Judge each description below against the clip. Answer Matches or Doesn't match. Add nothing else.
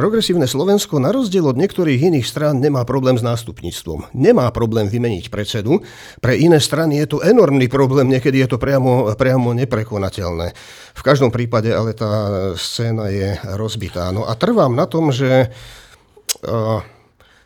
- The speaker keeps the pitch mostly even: Doesn't match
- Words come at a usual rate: Matches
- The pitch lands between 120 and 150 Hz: Matches